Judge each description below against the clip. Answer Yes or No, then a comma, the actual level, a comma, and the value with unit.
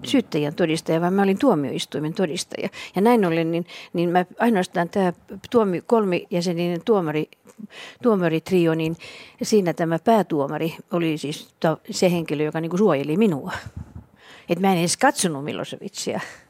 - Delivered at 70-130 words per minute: No, average, 140 wpm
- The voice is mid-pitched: Yes, medium, 175 Hz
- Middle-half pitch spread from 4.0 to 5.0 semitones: Yes, average, 4.4 semitones